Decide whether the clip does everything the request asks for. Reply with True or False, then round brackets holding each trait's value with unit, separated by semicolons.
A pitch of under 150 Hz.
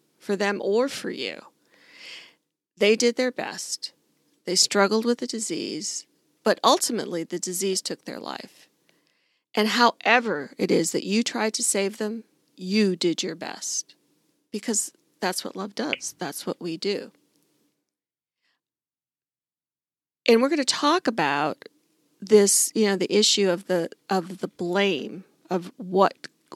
False (205 Hz)